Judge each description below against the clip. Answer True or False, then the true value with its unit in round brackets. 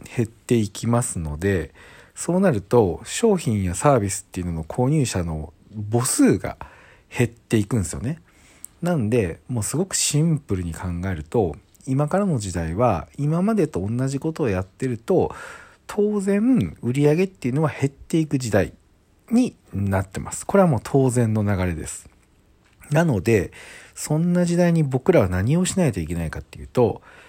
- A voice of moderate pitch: False (120 Hz)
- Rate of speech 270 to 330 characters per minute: True (320 characters per minute)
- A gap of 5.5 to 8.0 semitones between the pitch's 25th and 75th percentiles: False (8.6 semitones)